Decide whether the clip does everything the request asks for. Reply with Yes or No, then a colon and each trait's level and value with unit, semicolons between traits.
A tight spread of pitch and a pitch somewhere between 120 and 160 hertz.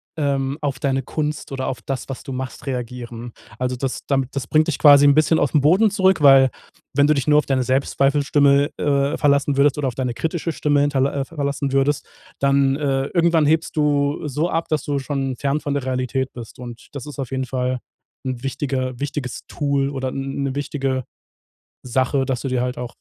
Yes: narrow, 1.9 semitones; medium, 140 Hz